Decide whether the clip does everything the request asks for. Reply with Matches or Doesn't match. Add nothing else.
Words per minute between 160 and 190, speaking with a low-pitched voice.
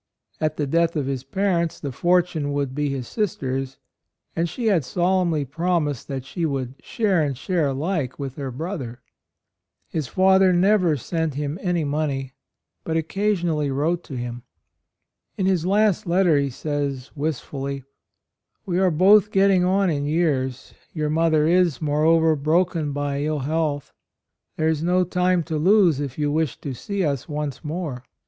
Doesn't match